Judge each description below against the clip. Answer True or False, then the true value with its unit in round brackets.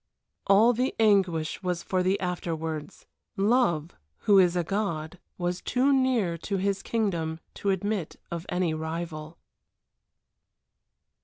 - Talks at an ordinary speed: False (125 wpm)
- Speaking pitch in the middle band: True (180 Hz)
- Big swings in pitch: False (3.6 semitones)